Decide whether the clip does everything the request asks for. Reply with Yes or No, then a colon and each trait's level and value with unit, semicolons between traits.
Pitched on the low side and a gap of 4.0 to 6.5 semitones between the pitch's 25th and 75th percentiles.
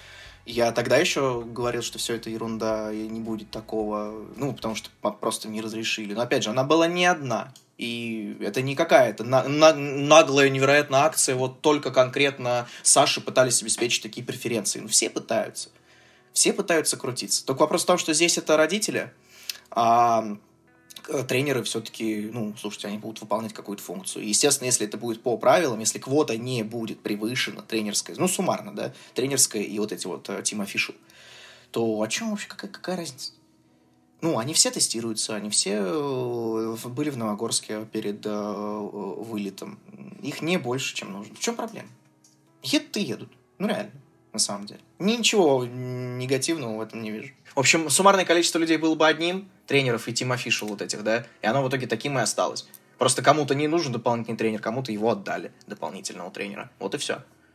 Yes: low, 120 Hz; average, 4.7 semitones